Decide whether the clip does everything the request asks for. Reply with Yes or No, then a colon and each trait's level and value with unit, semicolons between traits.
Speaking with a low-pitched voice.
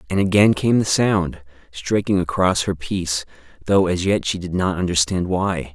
Yes: very low, 90 Hz